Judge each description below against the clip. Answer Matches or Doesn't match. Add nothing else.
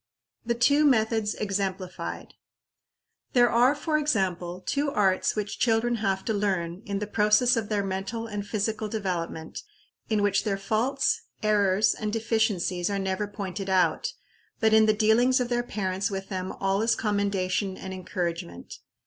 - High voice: Matches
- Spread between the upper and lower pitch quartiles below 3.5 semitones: Matches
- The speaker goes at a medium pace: Matches